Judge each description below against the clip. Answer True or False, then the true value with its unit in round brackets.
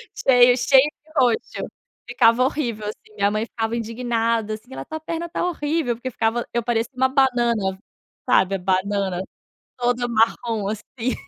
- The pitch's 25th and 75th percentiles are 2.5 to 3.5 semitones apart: True (2.8 semitones)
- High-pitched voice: True (235 Hz)